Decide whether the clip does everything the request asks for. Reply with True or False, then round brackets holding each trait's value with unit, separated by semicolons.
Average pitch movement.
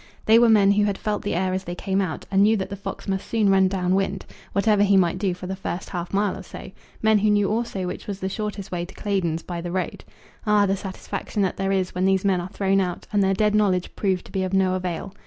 False (1.7 semitones)